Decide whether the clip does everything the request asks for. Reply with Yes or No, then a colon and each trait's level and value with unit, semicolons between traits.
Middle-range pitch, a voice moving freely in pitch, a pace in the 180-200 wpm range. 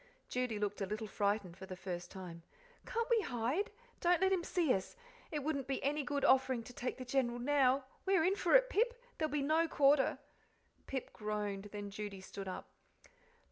No: very high, 260 Hz; wide, 7.1 semitones; average, 195 wpm